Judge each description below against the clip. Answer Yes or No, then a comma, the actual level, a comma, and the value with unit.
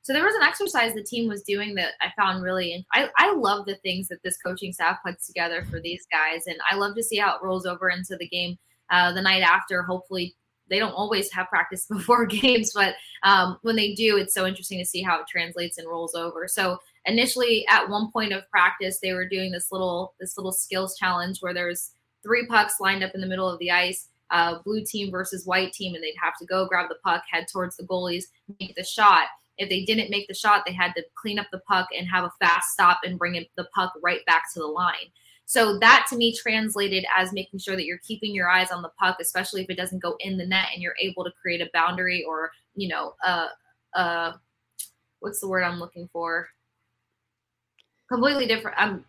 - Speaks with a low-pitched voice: No, medium, 185 Hz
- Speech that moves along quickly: Yes, fast, 230 wpm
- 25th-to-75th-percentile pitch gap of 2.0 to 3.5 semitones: Yes, narrow, 2.4 semitones